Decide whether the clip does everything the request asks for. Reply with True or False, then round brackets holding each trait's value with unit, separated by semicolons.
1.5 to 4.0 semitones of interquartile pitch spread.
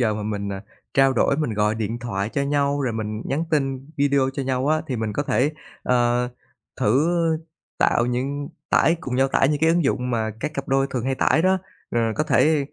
True (3.5 semitones)